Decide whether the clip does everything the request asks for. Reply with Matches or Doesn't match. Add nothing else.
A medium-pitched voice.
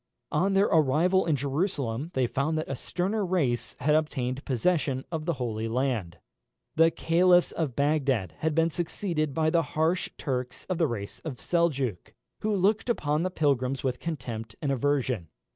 Matches